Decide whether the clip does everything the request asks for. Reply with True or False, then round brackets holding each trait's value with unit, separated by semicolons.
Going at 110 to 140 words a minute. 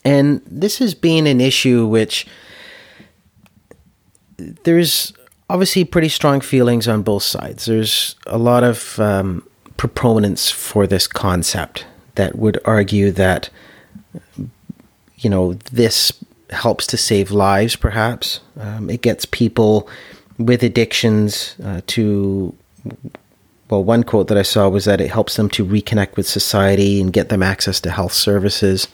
True (135 wpm)